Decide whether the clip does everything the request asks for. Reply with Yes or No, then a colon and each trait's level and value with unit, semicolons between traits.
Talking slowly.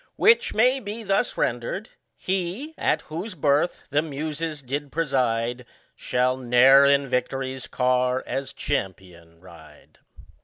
Yes: slow, 120 wpm